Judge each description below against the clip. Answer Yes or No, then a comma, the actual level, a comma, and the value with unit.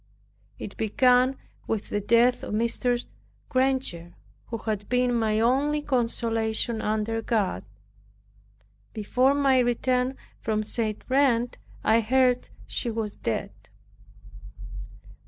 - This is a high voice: Yes, high, 235 Hz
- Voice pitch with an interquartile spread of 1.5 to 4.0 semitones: Yes, average, 2.7 semitones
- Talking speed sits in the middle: No, slow, 105 wpm